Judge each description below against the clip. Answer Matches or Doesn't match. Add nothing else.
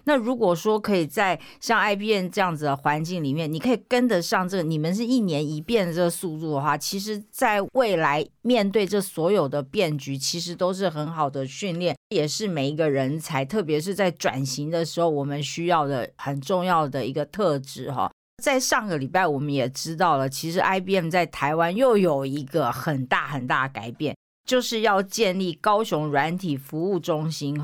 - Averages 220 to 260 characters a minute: Doesn't match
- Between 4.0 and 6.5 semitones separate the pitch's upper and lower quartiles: Matches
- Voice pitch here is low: Doesn't match